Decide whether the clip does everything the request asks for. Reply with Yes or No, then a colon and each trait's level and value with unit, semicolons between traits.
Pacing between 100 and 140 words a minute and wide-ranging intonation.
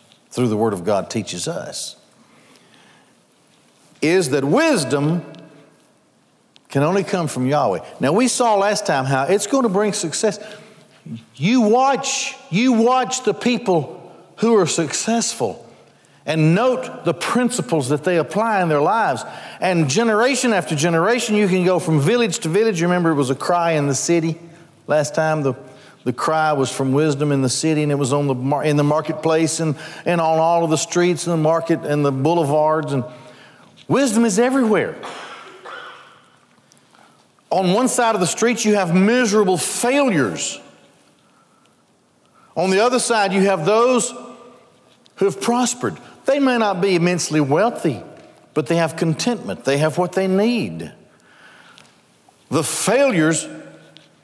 No: average, 155 wpm; wide, 6.5 semitones